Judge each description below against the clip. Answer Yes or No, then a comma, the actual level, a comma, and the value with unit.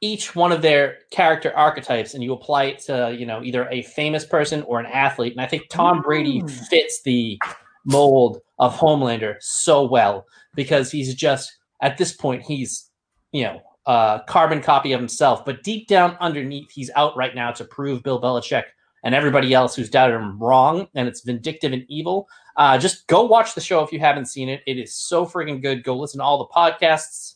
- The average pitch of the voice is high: No, medium, 140 Hz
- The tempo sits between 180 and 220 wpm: Yes, average, 200 wpm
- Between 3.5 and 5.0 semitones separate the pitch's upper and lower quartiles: Yes, average, 3.8 semitones